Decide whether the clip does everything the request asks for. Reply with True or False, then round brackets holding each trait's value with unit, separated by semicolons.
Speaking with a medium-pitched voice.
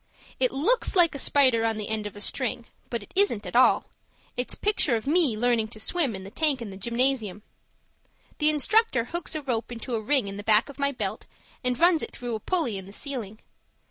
False (245 Hz)